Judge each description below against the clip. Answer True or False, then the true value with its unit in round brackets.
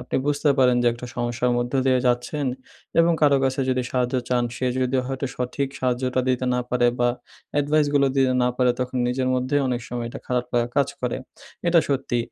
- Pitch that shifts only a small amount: True (1.8 semitones)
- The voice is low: True (125 Hz)